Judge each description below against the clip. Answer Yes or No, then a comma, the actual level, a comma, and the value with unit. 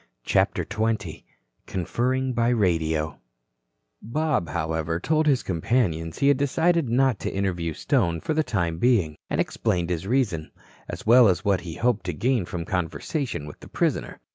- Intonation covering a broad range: Yes, wide, 7.3 semitones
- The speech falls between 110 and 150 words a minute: No, average, 160 wpm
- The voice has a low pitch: Yes, low, 100 Hz